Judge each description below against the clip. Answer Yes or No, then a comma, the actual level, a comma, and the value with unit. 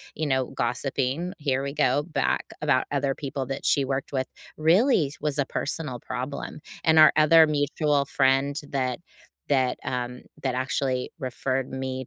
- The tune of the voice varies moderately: No, narrow, 2.3 semitones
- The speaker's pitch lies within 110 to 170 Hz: Yes, medium, 140 Hz